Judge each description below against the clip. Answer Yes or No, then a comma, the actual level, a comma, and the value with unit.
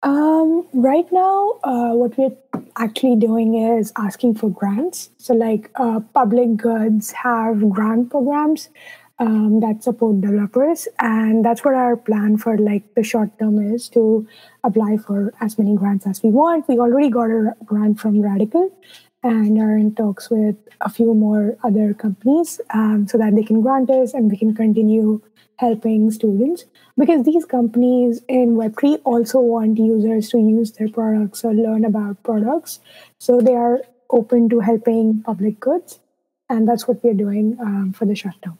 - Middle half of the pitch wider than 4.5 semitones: No, narrow, 2.5 semitones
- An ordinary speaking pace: Yes, average, 170 wpm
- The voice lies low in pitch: No, high, 230 Hz